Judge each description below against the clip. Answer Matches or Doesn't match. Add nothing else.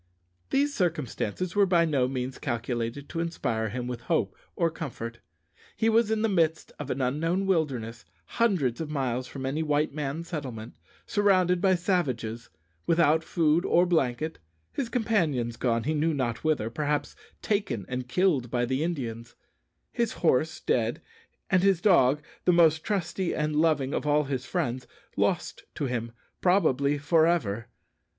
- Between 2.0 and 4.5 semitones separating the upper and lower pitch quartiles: Doesn't match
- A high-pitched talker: Doesn't match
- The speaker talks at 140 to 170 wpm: Matches